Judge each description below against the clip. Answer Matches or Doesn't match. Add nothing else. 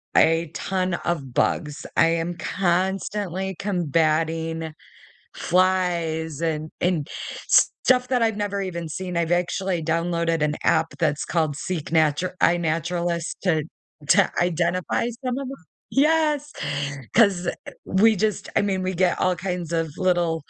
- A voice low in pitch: Doesn't match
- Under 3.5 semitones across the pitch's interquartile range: Matches